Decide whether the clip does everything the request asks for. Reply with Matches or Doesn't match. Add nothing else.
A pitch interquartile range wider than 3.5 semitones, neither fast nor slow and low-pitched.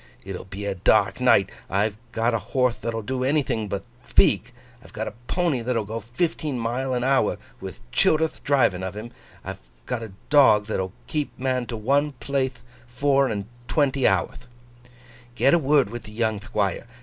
Matches